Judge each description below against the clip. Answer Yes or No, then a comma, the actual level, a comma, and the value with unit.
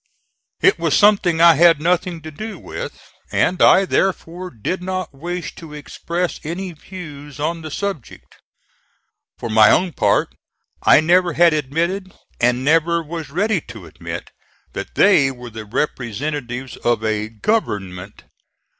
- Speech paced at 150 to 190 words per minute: No, average, 140 wpm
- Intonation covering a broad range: Yes, wide, 5.7 semitones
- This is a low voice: No, medium, 160 Hz